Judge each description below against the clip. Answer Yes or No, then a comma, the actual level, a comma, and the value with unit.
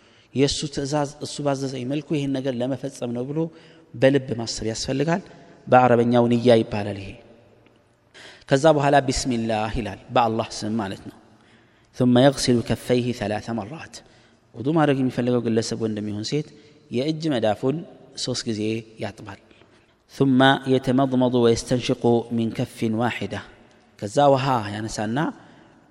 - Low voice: Yes, low, 120 Hz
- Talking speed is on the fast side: Yes, fast, 130 wpm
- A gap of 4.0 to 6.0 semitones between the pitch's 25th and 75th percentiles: No, average, 3.1 semitones